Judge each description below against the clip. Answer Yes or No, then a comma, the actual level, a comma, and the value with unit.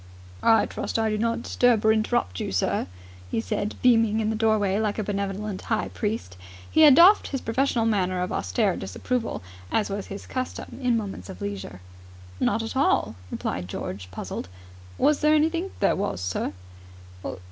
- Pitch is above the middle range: Yes, high, 215 Hz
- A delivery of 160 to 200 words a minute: Yes, average, 175 wpm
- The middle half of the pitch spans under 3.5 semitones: No, average, 4.0 semitones